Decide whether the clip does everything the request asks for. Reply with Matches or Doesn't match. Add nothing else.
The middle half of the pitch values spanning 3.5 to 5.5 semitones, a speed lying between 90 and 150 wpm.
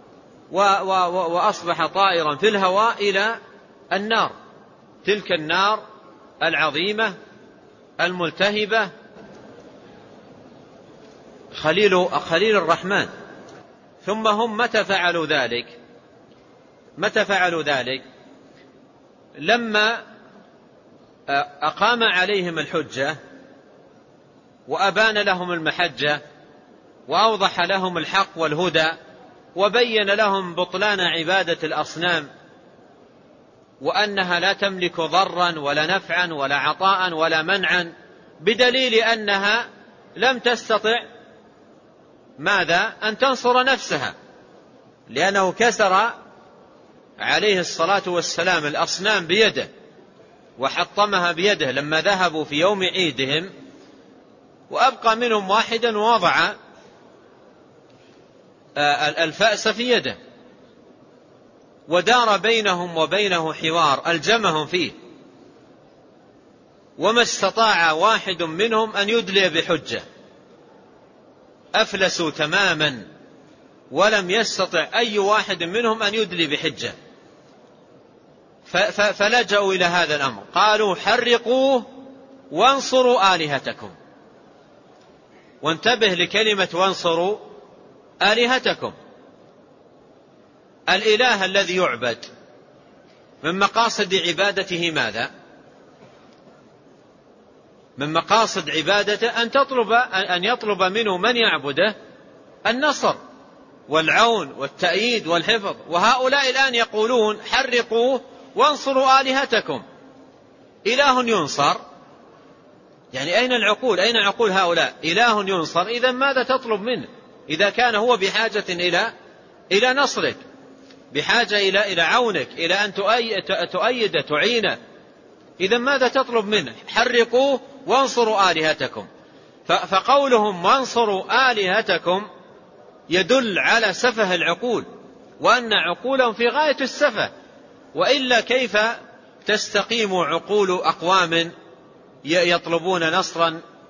Doesn't match